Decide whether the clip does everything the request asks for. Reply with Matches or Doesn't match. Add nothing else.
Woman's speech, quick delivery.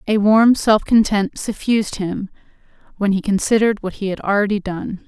Doesn't match